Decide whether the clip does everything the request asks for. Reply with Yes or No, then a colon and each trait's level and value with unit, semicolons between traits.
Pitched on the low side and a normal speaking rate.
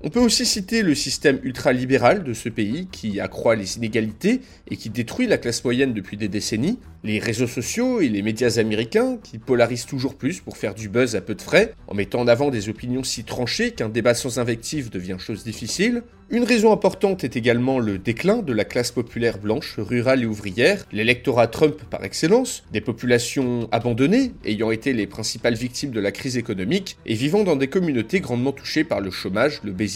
Yes: low, 120 Hz; average, 200 wpm